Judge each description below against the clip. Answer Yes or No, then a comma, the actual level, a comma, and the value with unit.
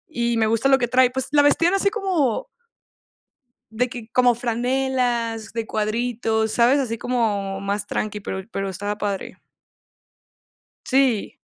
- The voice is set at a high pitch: Yes, high, 235 Hz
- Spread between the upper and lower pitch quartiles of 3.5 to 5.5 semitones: No, average, 3.1 semitones